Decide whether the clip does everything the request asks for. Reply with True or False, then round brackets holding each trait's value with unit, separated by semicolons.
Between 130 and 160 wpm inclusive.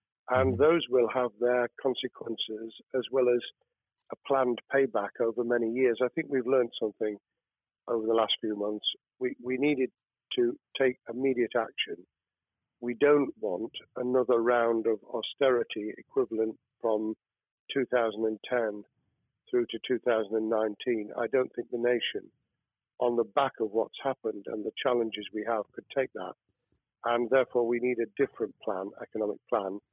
True (145 wpm)